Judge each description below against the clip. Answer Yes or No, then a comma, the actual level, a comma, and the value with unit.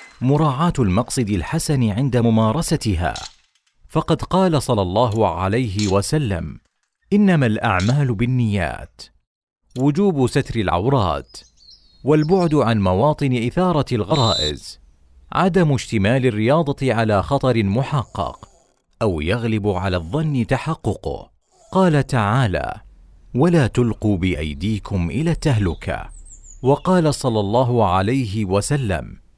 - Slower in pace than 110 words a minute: Yes, average, 90 wpm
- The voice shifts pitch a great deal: Yes, wide, 6.4 semitones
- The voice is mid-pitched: No, low, 120 Hz